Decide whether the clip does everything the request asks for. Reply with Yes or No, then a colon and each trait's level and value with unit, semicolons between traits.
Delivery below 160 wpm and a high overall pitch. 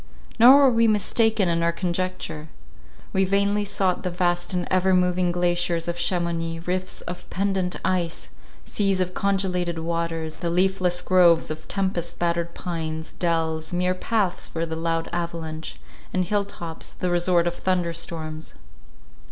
No: average, 150 wpm; medium, 175 Hz